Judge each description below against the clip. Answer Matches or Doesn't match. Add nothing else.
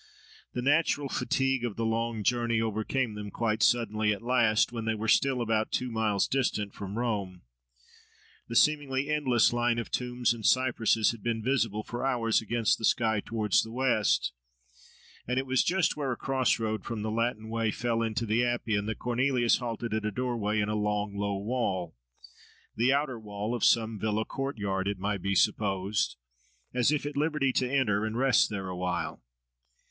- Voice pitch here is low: Matches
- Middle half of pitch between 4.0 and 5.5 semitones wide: Doesn't match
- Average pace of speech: Matches